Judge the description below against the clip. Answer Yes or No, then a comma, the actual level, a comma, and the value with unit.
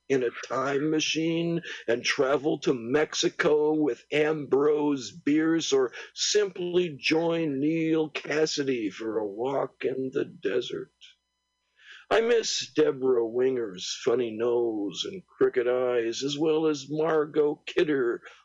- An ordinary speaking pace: No, slow, 115 wpm